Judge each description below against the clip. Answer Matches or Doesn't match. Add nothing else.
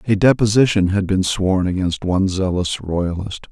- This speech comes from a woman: Doesn't match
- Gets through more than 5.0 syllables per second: Doesn't match